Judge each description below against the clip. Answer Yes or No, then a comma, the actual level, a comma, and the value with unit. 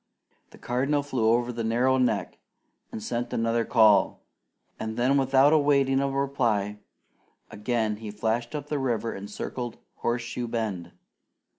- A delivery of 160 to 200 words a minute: No, slow, 135 wpm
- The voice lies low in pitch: Yes, low, 120 Hz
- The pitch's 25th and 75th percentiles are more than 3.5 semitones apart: No, average, 3.2 semitones